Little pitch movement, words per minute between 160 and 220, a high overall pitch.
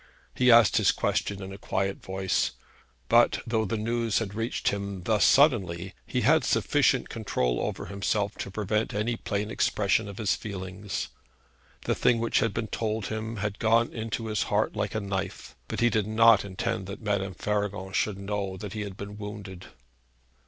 No: narrow, 2.3 semitones; average, 180 wpm; low, 105 Hz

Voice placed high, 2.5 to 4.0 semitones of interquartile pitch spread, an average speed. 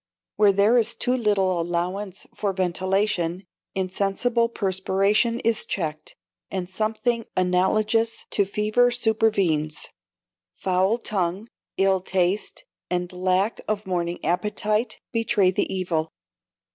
No: high, 195 Hz; average, 3.0 semitones; slow, 105 wpm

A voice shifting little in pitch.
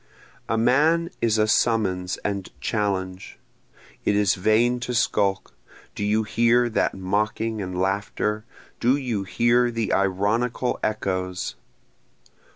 No: average, 3.4 semitones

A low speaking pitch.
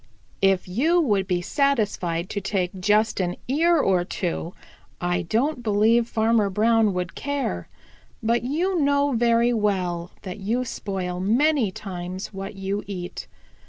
No: high, 205 Hz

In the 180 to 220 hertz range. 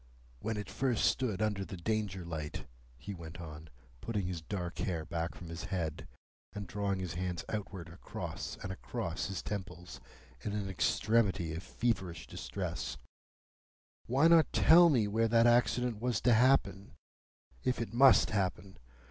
No: low, 100 Hz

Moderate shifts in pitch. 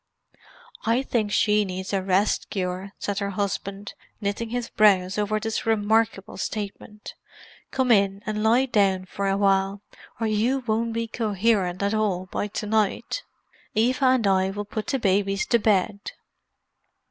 No: narrow, 2.2 semitones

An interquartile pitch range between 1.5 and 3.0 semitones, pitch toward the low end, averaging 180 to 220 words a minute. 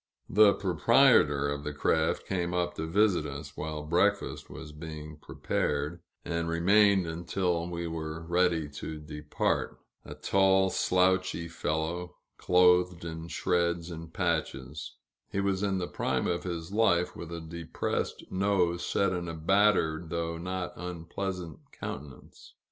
No: narrow, 2.5 semitones; very low, 85 Hz; slow, 135 wpm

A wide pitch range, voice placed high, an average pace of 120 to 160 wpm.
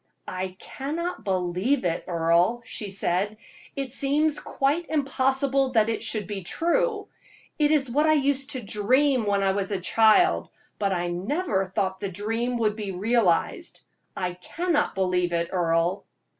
Yes: wide, 6.7 semitones; high, 215 Hz; average, 145 wpm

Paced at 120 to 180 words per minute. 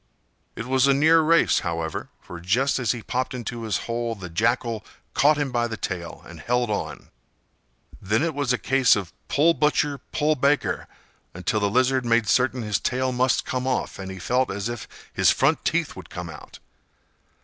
No: average, 190 wpm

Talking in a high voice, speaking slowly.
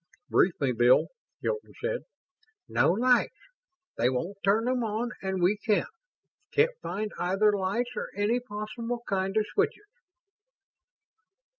Yes: high, 215 Hz; slow, 130 wpm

